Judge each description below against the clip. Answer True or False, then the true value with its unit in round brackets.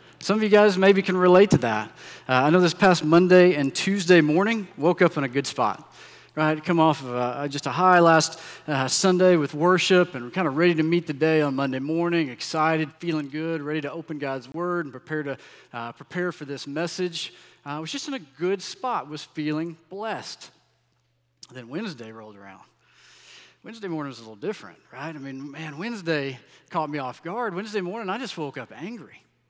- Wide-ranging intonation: False (4.2 semitones)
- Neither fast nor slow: False (210 wpm)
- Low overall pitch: False (160 Hz)